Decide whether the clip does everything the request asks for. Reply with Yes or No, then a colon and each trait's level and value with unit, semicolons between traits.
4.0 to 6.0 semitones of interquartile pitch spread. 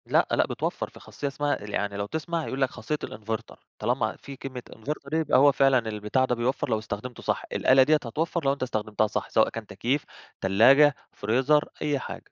Yes: average, 4.7 semitones